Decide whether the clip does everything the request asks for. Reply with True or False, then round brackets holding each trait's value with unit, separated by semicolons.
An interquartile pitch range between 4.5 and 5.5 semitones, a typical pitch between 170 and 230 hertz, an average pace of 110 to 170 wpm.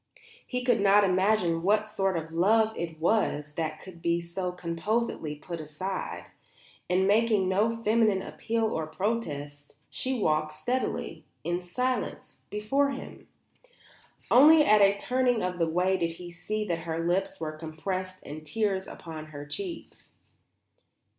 True (4.8 semitones; 185 Hz; 145 wpm)